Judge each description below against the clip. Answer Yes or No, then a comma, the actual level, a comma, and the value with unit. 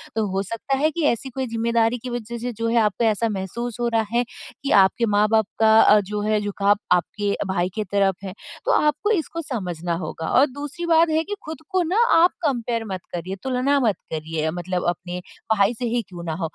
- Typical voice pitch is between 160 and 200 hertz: No, high, 225 Hz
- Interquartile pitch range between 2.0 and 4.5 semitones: No, wide, 5.6 semitones